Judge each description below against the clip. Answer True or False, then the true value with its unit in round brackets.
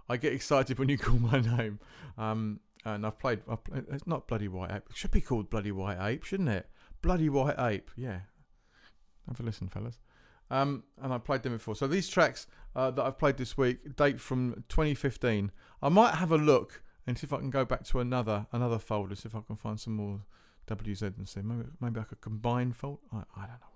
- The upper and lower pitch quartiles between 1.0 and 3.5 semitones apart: False (4.2 semitones)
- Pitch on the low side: True (120 Hz)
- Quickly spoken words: True (225 wpm)